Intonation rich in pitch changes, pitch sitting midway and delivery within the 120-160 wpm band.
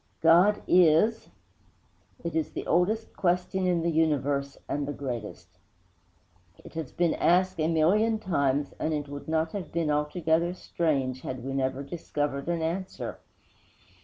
No: average, 3.8 semitones; medium, 160 Hz; average, 155 wpm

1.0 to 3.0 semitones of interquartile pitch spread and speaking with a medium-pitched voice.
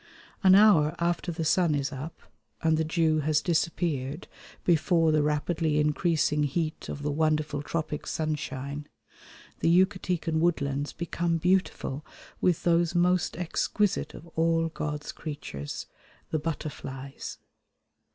Yes: narrow, 2.4 semitones; medium, 160 Hz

